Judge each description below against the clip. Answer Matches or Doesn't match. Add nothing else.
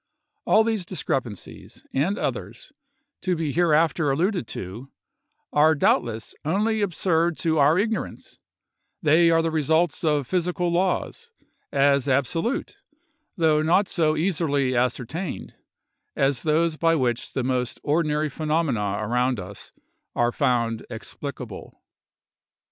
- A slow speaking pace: Matches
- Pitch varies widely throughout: Doesn't match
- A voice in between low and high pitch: Matches